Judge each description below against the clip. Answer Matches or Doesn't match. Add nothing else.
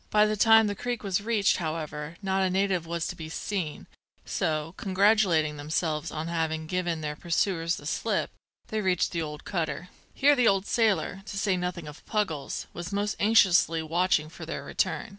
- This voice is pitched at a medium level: Matches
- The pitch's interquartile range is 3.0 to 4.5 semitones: Matches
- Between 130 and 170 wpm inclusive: Doesn't match